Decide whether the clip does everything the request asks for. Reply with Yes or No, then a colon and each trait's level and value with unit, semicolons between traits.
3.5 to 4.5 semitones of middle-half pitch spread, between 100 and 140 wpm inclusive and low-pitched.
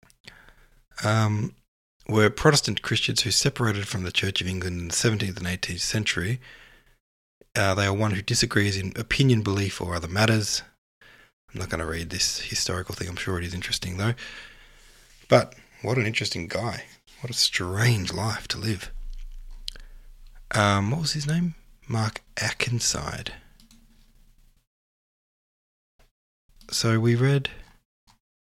Yes: average, 4.1 semitones; slow, 135 wpm; low, 105 Hz